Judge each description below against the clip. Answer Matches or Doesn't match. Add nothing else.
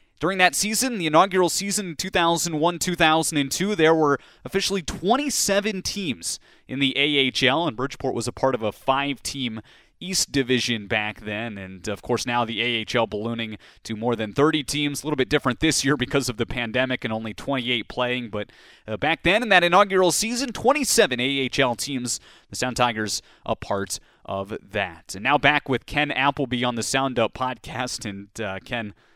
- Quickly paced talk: Doesn't match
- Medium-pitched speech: Doesn't match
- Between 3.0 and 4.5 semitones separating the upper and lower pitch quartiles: Doesn't match